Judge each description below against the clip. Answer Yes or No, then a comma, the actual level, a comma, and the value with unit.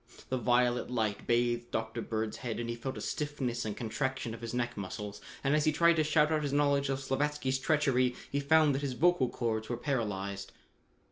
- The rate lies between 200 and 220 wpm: Yes, fast, 205 wpm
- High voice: No, low, 125 Hz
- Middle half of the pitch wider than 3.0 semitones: Yes, average, 3.6 semitones